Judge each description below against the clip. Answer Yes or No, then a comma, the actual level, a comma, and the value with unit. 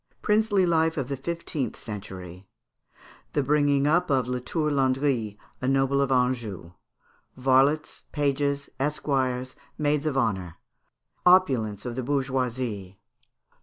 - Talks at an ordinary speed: No, slow, 115 wpm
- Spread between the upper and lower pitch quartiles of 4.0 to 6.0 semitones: No, average, 3.1 semitones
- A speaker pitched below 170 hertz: Yes, low, 135 Hz